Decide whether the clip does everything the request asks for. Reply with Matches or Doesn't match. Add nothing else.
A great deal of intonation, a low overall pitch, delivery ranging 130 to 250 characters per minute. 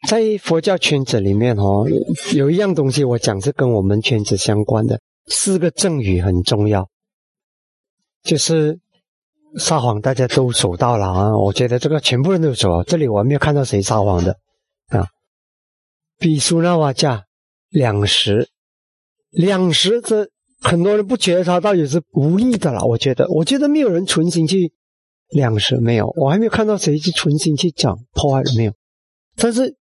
Doesn't match